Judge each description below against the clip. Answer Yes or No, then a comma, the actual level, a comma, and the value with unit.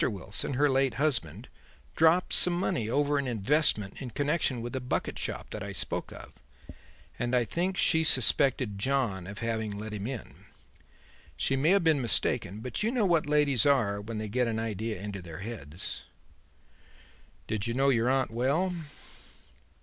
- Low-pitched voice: Yes, low, 125 Hz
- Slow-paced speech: No, average, 170 wpm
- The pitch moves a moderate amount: Yes, average, 5.0 semitones